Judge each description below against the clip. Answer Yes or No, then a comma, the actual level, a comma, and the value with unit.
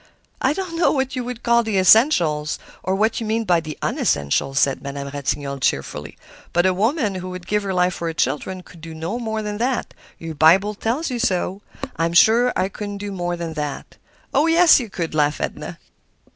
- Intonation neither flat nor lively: No, wide, 6.0 semitones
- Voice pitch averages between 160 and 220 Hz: Yes, high, 190 Hz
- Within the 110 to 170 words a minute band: No, average, 200 wpm